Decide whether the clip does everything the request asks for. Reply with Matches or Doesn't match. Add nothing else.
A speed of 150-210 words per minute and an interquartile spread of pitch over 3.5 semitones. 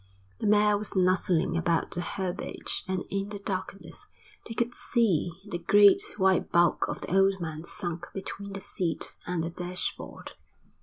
Doesn't match